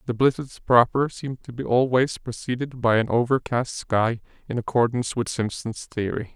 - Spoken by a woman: No, male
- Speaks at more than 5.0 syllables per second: No, 4.9 syllables/s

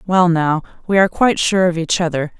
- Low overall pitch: No, medium, 175 Hz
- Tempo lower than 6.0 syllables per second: No, 6.1 syllables/s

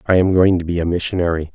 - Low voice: Yes, very low, 90 Hz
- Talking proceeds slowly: No, fast, 270 wpm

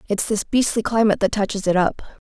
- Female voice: Yes, female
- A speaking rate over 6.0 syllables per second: Yes, 6.4 syllables/s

